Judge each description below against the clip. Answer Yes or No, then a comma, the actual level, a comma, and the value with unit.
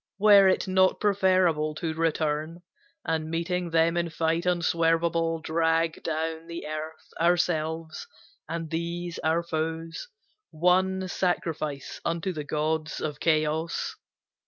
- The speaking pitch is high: No, medium, 165 Hz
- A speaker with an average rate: No, slow, 115 wpm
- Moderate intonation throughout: No, narrow, 1.6 semitones